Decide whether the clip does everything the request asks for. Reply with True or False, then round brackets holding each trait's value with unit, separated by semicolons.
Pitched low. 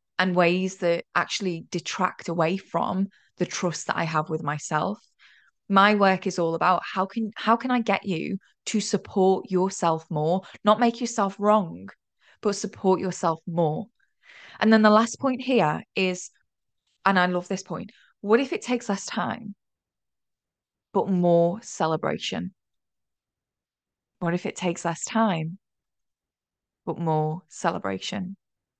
False (185 Hz)